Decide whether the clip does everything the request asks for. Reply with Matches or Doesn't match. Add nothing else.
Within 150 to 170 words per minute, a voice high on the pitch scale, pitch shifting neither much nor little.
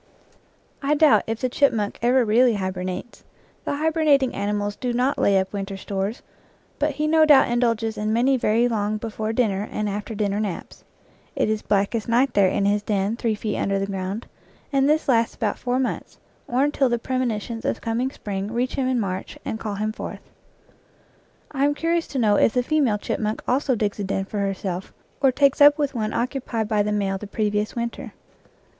Doesn't match